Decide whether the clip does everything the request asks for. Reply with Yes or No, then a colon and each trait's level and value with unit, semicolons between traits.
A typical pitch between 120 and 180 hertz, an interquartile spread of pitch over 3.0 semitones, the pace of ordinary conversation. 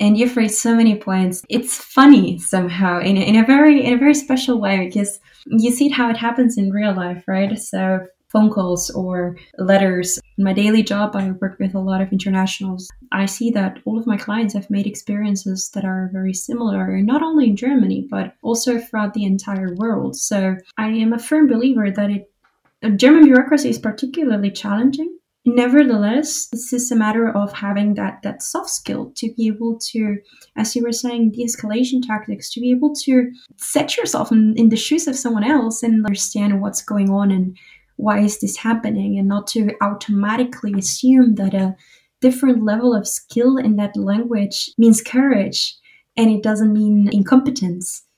No: high, 215 Hz; average, 3.6 semitones; average, 185 wpm